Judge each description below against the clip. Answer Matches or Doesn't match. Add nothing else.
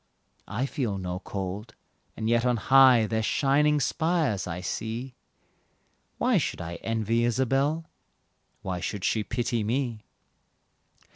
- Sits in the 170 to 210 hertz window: Doesn't match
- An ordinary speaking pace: Doesn't match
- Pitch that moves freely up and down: Doesn't match